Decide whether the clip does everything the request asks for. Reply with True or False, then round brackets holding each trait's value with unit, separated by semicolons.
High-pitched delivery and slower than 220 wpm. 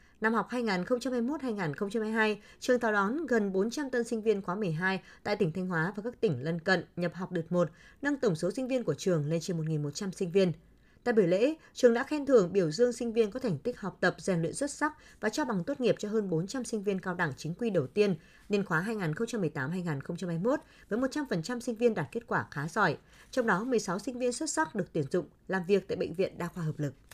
False (205 Hz; 230 wpm)